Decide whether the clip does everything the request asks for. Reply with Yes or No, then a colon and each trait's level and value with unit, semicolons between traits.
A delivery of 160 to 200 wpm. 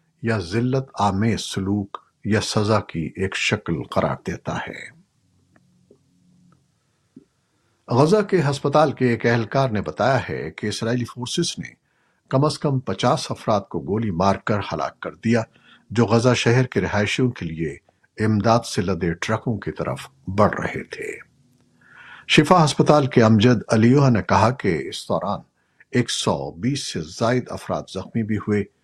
No: average, 150 wpm